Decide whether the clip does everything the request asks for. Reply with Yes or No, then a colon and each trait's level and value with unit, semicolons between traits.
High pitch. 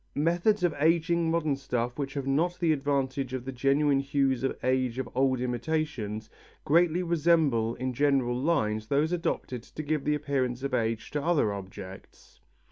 No: medium, 140 Hz